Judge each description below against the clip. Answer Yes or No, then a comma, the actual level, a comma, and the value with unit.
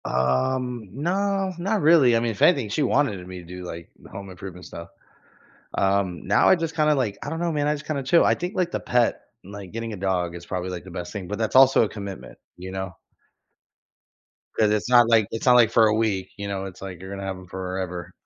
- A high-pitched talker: No, low, 105 Hz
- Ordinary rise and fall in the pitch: No, wide, 6.1 semitones